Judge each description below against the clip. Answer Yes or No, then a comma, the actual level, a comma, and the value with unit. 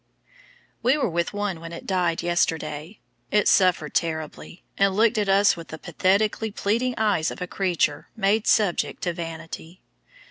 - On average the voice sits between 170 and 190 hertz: Yes, medium, 185 Hz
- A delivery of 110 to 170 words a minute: Yes, average, 155 wpm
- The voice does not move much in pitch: No, average, 3.8 semitones